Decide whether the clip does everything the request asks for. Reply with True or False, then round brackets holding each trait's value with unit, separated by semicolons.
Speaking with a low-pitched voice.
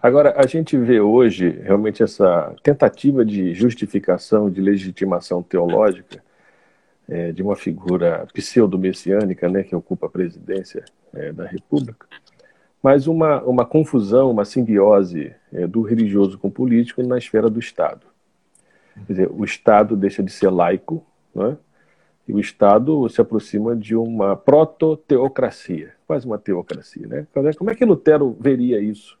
True (115 Hz)